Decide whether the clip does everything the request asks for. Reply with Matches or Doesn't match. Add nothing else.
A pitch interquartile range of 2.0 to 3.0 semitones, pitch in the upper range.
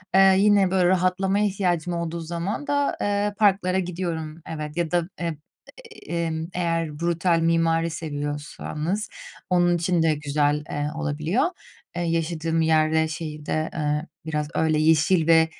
Doesn't match